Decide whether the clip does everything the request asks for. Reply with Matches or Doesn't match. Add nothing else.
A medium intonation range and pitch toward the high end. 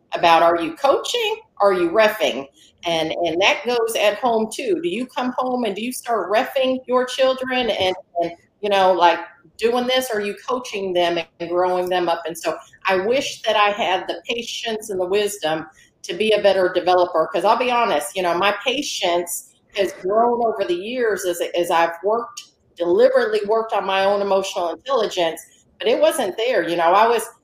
Doesn't match